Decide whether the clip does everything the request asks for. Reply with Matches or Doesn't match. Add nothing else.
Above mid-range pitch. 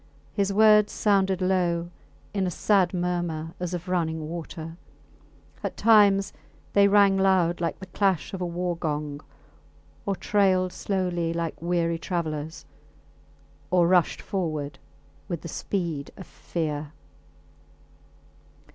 Doesn't match